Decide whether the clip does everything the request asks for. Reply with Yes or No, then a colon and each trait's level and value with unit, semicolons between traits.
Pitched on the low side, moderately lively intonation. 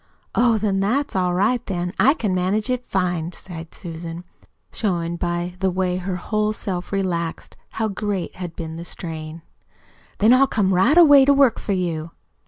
No: medium, 185 Hz; average, 3.8 semitones